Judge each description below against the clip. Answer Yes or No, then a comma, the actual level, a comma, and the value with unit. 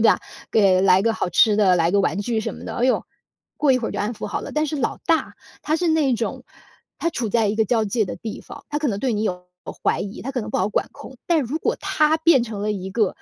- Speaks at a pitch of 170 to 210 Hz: No, high, 225 Hz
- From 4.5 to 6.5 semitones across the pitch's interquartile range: Yes, average, 5.2 semitones